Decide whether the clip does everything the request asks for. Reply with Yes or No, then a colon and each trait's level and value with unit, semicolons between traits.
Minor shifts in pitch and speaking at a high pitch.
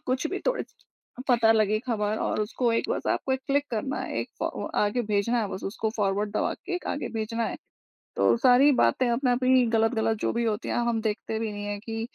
No: average, 3.0 semitones; high, 230 Hz